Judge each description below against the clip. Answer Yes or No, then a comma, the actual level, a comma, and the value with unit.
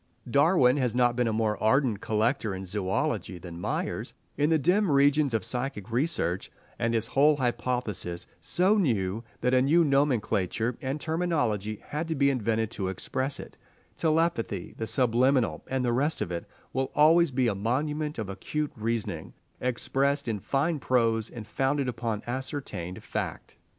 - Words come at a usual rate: Yes, average, 160 wpm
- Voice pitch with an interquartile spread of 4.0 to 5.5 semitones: Yes, average, 4.7 semitones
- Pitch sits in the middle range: No, low, 125 Hz